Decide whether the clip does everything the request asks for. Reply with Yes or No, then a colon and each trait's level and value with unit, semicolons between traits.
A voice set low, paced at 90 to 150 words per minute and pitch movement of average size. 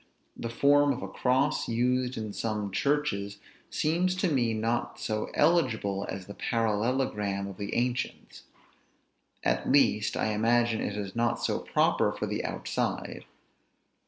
Yes: low, 115 Hz; average, 140 wpm; average, 4.0 semitones